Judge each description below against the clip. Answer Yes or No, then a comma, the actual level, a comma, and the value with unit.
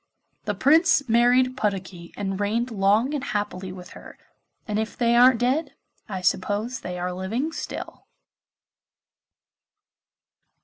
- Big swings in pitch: No, average, 4.7 semitones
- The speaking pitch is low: No, high, 220 Hz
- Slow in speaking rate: Yes, slow, 125 wpm